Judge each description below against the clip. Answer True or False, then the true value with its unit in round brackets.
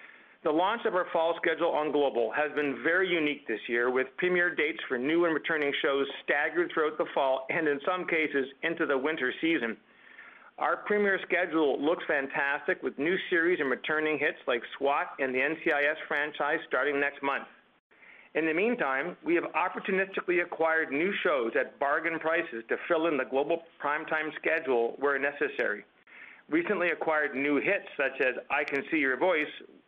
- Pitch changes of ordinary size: True (3.5 semitones)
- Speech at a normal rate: True (175 wpm)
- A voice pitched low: False (155 Hz)